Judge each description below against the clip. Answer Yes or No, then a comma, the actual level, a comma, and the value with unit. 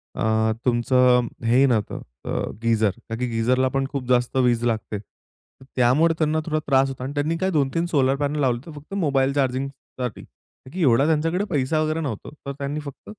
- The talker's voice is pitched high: No, low, 135 Hz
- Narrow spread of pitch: No, average, 3.3 semitones